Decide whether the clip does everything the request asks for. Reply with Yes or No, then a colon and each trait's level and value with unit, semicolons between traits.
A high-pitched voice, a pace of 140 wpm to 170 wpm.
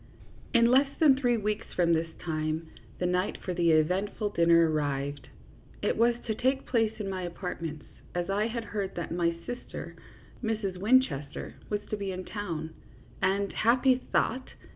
Yes: high, 195 Hz; average, 165 wpm